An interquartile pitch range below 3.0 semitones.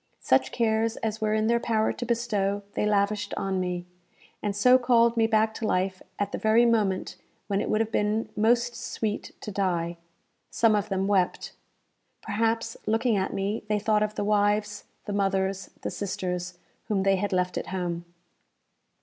Yes: narrow, 2.5 semitones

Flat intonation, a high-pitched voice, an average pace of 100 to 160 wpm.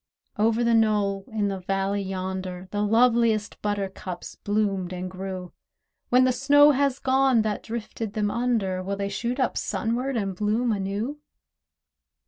No: average, 3.4 semitones; high, 210 Hz; average, 145 wpm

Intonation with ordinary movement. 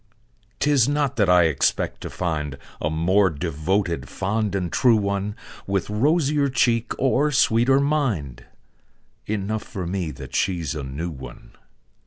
No: wide, 6.6 semitones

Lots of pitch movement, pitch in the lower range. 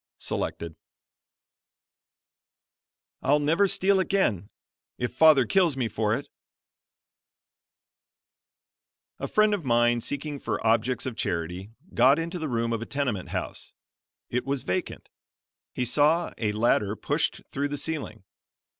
Yes: wide, 5.7 semitones; low, 130 Hz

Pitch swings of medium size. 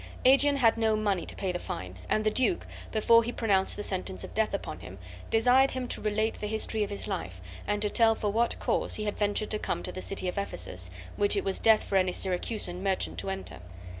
Yes: average, 3.3 semitones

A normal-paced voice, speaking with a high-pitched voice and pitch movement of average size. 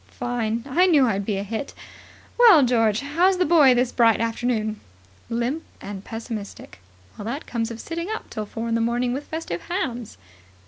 Yes: average, 175 wpm; high, 240 Hz; average, 4.5 semitones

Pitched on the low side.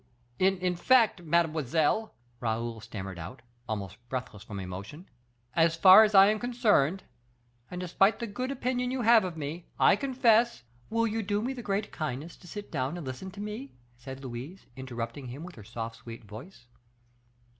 No: medium, 170 Hz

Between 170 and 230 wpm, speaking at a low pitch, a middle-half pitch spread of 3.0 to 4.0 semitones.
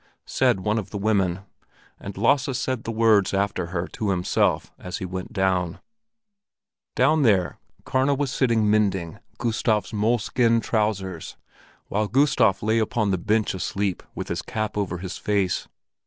No: average, 150 wpm; low, 105 Hz; average, 3.3 semitones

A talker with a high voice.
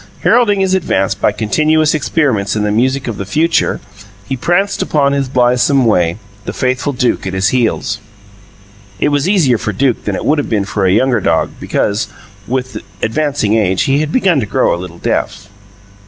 No: low, 125 Hz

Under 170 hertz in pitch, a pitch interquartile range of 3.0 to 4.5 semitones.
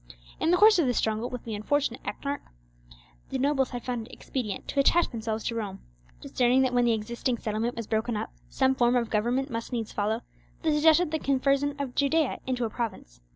No: high, 245 Hz; average, 3.7 semitones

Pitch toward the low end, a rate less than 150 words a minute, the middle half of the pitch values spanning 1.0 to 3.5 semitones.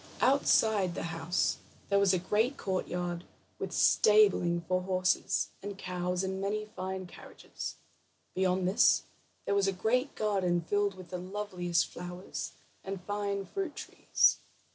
No: high, 190 Hz; average, 140 wpm; narrow, 2.4 semitones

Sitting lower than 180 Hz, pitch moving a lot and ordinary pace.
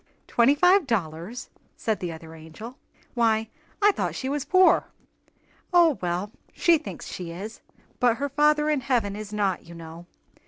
No: high, 225 Hz; wide, 8.3 semitones; average, 160 wpm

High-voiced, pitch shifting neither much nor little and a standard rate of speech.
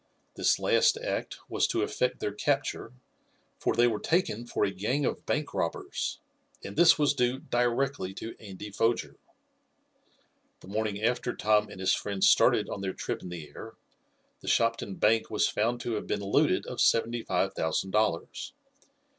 No: low, 115 Hz; average, 3.7 semitones; average, 170 wpm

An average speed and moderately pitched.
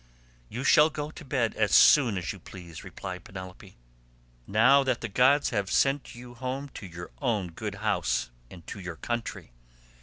No: average, 175 wpm; low, 110 Hz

